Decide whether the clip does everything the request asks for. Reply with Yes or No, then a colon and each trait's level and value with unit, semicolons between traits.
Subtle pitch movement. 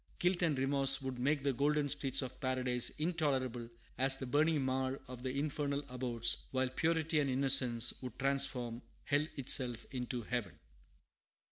Yes: narrow, 2.2 semitones